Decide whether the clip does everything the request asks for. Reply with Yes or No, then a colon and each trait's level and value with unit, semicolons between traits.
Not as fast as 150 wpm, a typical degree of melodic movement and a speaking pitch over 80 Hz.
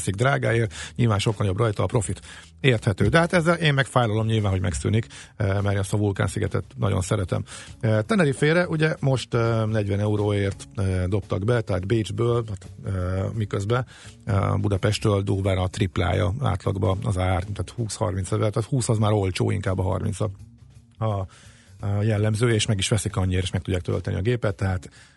No: fast, 155 wpm; average, 3.1 semitones; low, 105 Hz